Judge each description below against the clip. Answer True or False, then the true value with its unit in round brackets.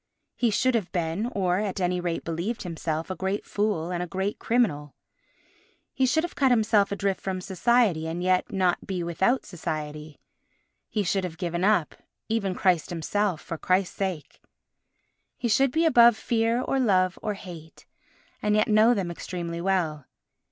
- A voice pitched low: False (190 Hz)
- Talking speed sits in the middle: True (170 wpm)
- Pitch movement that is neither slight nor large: True (3.9 semitones)